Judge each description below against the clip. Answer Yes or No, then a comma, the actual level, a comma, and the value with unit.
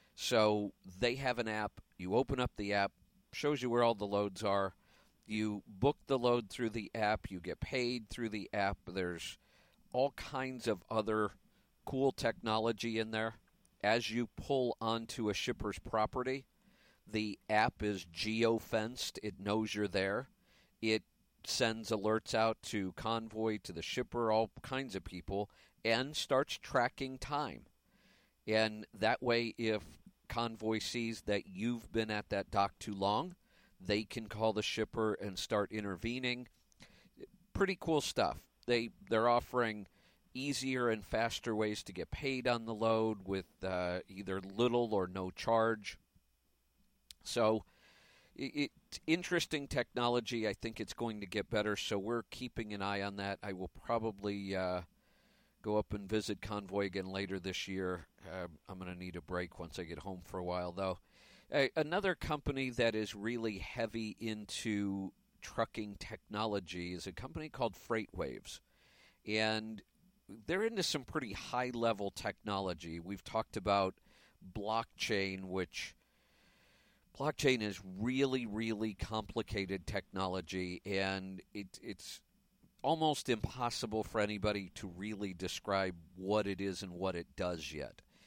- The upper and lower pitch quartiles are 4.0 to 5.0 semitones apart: No, average, 3.3 semitones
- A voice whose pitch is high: No, low, 110 Hz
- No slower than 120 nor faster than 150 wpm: Yes, average, 145 wpm